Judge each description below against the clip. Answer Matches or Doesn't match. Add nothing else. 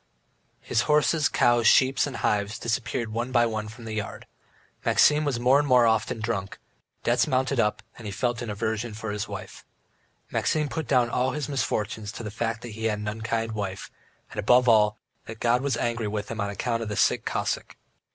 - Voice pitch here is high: Doesn't match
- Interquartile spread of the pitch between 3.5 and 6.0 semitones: Doesn't match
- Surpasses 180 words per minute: Matches